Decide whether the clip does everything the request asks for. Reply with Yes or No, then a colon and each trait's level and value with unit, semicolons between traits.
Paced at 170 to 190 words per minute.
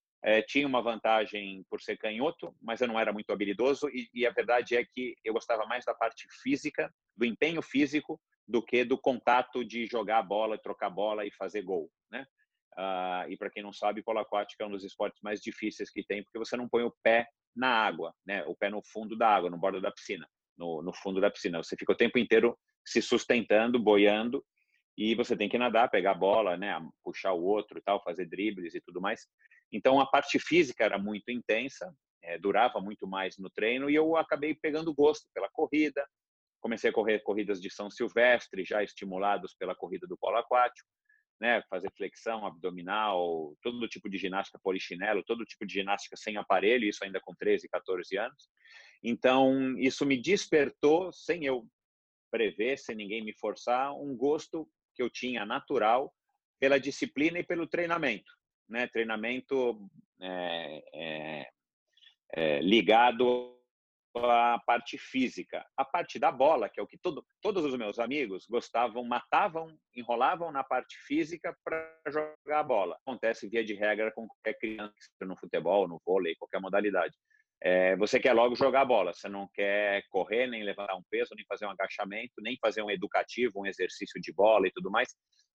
Yes: fast, 185 wpm